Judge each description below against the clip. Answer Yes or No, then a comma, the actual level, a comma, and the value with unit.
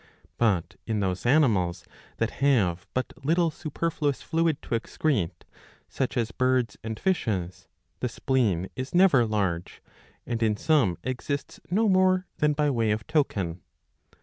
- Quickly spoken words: No, average, 140 wpm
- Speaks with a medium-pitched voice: No, low, 125 Hz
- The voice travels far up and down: Yes, wide, 6.3 semitones